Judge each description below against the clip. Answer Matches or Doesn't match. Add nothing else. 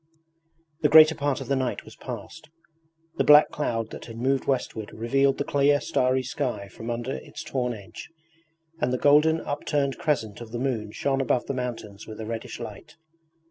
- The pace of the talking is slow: Doesn't match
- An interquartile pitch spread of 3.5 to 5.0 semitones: Matches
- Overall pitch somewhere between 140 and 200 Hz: Doesn't match